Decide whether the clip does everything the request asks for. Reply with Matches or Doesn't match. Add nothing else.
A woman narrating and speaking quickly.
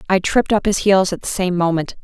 Matches